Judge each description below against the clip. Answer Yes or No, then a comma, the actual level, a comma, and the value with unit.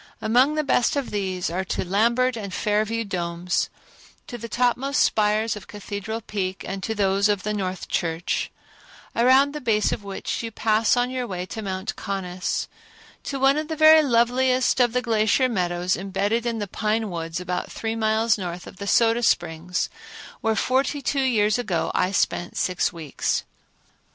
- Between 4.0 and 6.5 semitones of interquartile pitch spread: Yes, average, 4.3 semitones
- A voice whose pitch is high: Yes, high, 215 Hz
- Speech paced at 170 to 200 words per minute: Yes, average, 175 wpm